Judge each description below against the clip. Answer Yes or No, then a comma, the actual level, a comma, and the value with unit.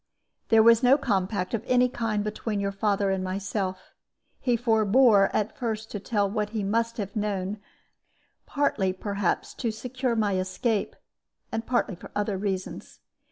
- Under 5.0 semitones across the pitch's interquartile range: Yes, average, 2.7 semitones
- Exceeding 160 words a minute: No, average, 155 wpm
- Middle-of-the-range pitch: No, high, 210 Hz